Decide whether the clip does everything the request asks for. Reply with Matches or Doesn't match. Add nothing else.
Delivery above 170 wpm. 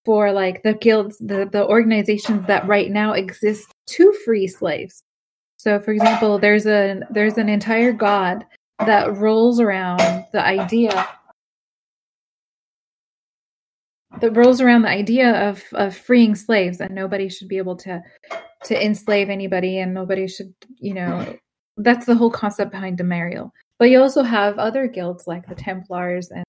Doesn't match